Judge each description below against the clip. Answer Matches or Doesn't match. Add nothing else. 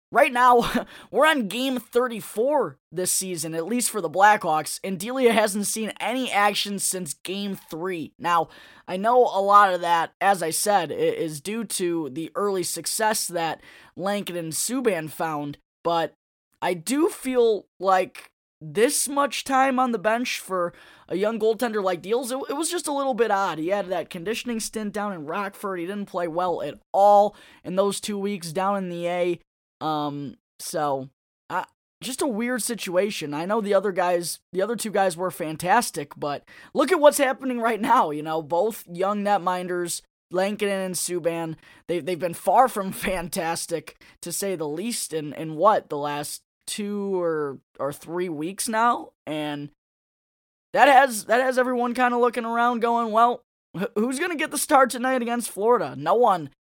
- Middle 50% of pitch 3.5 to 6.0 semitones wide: Matches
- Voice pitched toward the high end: Matches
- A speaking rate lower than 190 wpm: Matches